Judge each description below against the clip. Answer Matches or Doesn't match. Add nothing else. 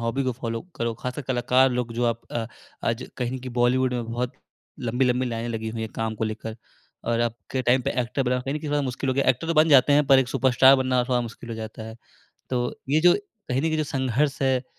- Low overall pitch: Matches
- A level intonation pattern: Matches